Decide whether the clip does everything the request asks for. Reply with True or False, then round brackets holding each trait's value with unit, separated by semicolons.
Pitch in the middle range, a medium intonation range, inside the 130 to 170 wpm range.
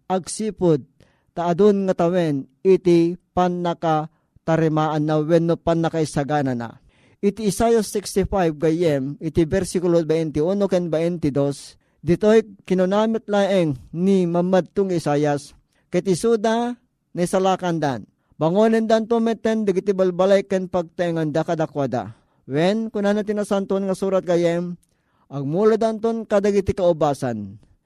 False (175 Hz; 4.3 semitones; 115 wpm)